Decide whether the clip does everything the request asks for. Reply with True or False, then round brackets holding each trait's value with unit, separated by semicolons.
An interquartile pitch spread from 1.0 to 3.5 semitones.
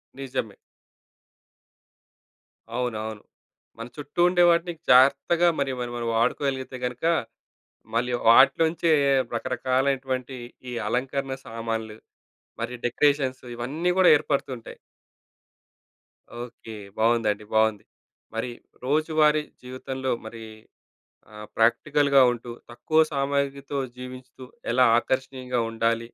True (3.2 semitones)